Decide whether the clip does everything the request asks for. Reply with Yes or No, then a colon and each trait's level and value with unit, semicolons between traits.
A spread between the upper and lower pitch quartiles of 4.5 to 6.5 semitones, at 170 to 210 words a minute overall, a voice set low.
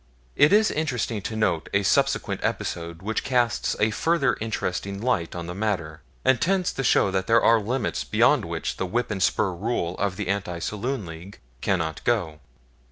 Yes: average, 5.2 semitones; average, 180 wpm; low, 105 Hz